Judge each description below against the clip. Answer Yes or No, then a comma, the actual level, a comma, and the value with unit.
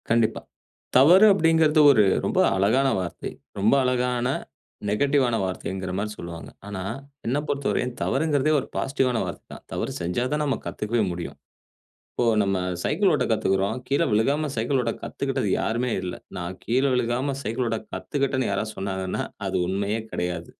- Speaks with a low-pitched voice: Yes, low, 120 Hz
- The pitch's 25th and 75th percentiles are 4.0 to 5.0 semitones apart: No, wide, 5.6 semitones